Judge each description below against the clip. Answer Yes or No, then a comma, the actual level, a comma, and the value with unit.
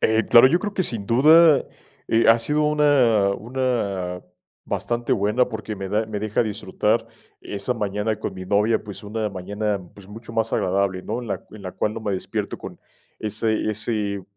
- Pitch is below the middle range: Yes, low, 110 Hz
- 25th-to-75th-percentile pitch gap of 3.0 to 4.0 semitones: No, narrow, 2.6 semitones